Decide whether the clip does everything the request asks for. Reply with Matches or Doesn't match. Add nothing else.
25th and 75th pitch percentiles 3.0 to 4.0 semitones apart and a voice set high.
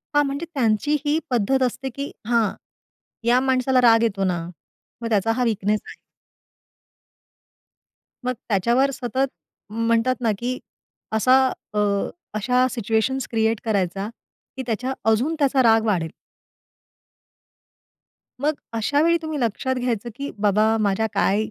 Matches